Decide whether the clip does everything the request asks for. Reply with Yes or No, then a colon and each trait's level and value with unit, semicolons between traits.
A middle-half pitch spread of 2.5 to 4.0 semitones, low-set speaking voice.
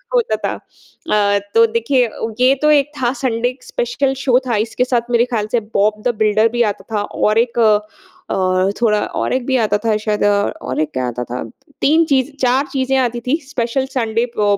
No: average, 3.6 semitones; high, 240 Hz